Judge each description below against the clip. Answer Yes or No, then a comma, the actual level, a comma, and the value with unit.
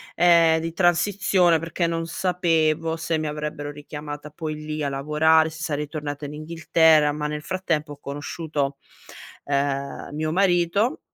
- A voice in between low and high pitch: Yes, medium, 155 Hz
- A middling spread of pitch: No, narrow, 2.1 semitones